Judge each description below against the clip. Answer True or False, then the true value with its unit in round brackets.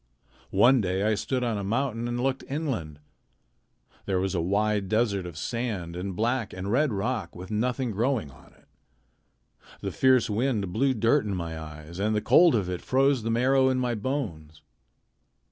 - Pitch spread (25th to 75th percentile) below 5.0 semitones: False (5.4 semitones)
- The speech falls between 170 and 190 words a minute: True (180 wpm)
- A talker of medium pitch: False (110 Hz)